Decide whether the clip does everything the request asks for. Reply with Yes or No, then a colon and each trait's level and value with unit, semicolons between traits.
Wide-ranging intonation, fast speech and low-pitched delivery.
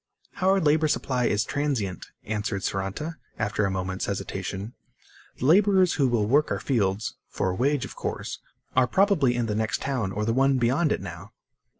No: wide, 6.3 semitones; average, 180 wpm; low, 120 Hz